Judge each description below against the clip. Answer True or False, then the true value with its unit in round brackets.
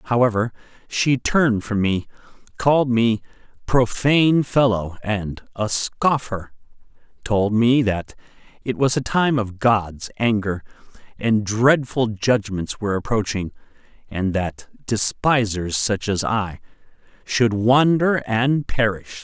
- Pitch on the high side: False (115 Hz)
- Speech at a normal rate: False (115 wpm)